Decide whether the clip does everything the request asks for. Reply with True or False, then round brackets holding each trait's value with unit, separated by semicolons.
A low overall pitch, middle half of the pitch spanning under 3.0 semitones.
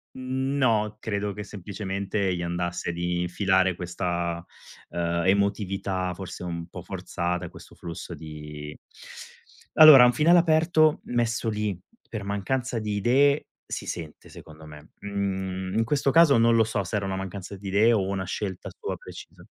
False (100 Hz; 4.3 semitones)